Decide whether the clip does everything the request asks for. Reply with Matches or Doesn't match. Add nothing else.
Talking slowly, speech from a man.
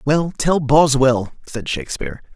Matches